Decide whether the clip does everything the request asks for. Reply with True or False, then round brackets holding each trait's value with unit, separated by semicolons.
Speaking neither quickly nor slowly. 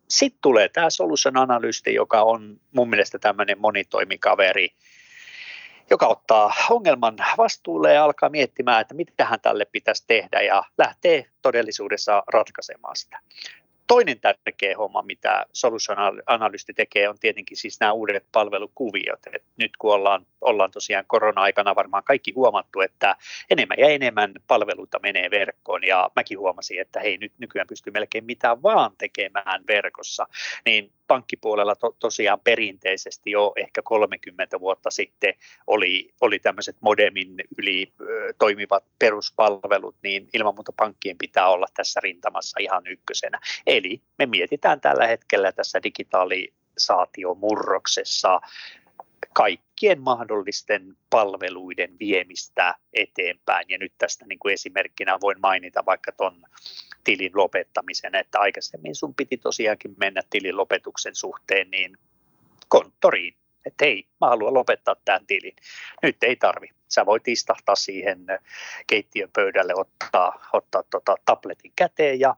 True (130 wpm)